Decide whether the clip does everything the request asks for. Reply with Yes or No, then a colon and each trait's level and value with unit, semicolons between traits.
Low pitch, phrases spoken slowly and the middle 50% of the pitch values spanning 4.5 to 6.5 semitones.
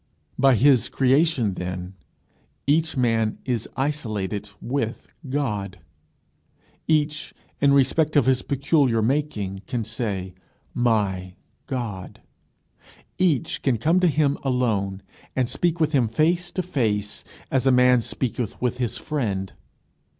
Yes: low, 125 Hz; slow, 120 wpm; average, 5.1 semitones